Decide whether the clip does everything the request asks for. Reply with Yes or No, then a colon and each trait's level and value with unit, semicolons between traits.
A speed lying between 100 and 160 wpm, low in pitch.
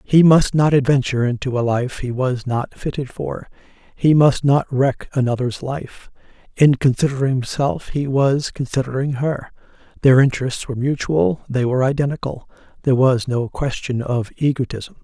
Yes: average, 150 wpm; low, 130 Hz